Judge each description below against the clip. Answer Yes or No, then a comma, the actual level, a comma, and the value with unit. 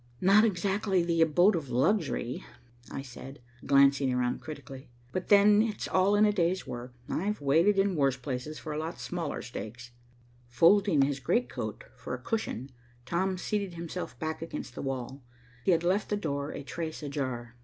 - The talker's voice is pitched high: No, medium, 160 Hz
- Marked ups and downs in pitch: Yes, wide, 6.0 semitones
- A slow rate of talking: No, average, 175 wpm